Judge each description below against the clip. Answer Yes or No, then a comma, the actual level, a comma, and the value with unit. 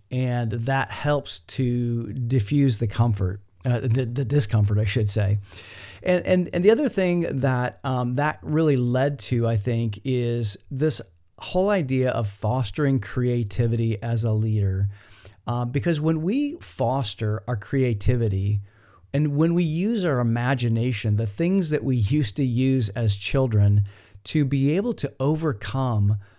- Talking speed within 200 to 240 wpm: No, average, 150 wpm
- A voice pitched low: Yes, low, 125 Hz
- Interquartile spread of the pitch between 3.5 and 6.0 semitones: Yes, average, 4.7 semitones